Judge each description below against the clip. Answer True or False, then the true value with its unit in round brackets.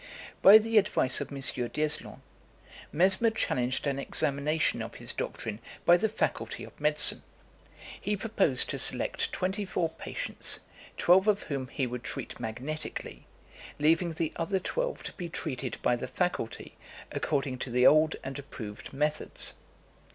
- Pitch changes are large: True (6.3 semitones)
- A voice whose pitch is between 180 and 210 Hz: False (155 Hz)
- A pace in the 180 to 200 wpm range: False (145 wpm)